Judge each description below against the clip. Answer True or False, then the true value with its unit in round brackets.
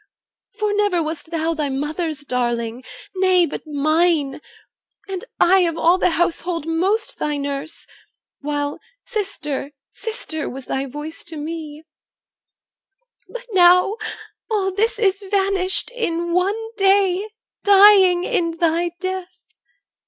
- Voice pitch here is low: False (345 Hz)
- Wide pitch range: False (4.1 semitones)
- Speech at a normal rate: False (120 wpm)